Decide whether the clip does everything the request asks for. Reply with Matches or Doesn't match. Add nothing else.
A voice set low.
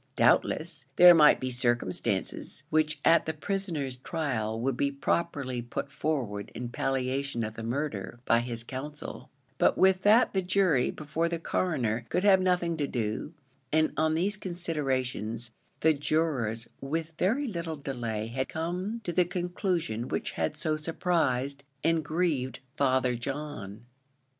Doesn't match